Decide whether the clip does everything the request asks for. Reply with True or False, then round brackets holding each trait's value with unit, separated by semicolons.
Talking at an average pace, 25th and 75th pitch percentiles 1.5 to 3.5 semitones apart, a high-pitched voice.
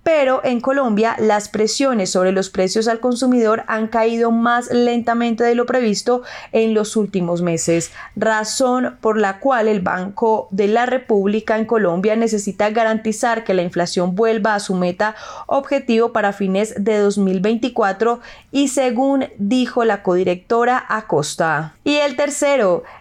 True (145 wpm; 3.2 semitones; 220 Hz)